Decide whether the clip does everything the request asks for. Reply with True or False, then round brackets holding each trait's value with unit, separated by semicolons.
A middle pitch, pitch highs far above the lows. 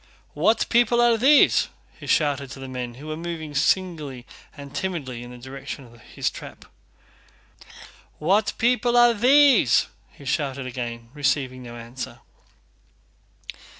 True (145 Hz; 8.4 semitones)